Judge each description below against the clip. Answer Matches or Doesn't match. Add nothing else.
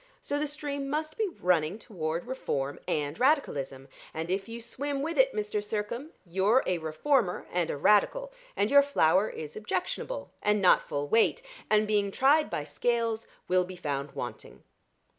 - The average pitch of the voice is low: Doesn't match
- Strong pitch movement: Matches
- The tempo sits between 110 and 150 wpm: Doesn't match